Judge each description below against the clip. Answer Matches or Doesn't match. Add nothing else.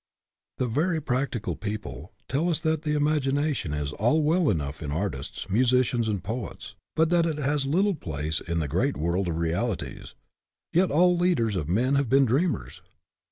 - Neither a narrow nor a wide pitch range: Doesn't match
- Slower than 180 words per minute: Matches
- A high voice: Doesn't match